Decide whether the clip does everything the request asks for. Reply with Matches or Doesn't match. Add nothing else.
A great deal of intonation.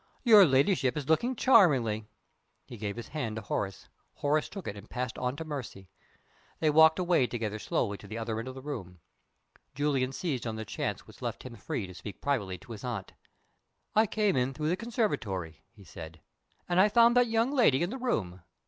Matches